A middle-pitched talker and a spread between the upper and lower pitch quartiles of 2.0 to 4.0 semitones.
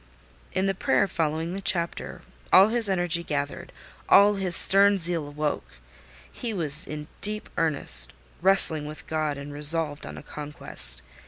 No: medium, 165 Hz; average, 4.5 semitones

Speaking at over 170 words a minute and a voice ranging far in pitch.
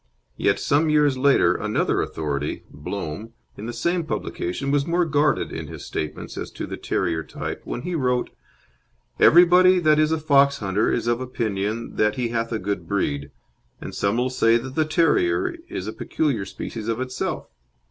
Yes: average, 180 wpm; wide, 6.4 semitones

